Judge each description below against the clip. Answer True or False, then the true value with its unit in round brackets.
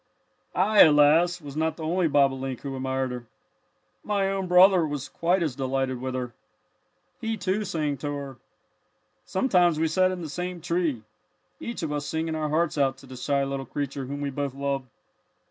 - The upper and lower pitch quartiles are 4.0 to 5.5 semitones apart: True (4.5 semitones)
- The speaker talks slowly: False (180 wpm)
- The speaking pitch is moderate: True (150 Hz)